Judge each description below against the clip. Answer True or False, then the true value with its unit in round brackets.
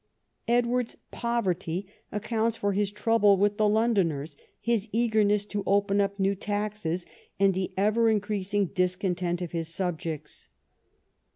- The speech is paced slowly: True (125 wpm)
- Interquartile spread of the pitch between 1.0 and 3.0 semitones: True (2.7 semitones)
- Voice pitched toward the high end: True (205 Hz)